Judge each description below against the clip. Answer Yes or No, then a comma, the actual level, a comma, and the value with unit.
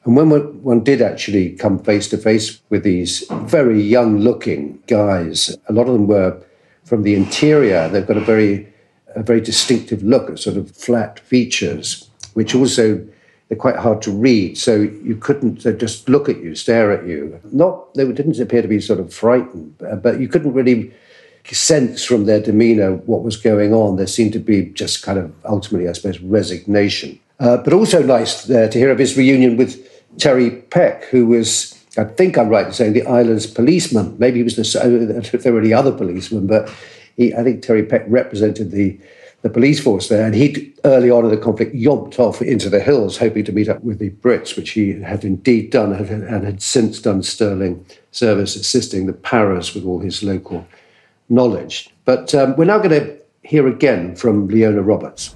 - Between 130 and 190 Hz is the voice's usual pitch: No, low, 110 Hz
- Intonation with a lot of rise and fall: No, average, 3.2 semitones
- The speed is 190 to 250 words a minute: Yes, average, 195 wpm